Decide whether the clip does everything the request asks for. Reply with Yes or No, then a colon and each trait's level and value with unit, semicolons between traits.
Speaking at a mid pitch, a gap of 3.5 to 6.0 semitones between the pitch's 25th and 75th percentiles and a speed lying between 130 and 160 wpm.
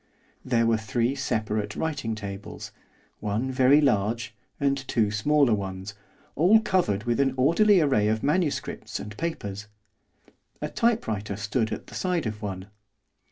No: low, 115 Hz; average, 5.2 semitones; average, 140 wpm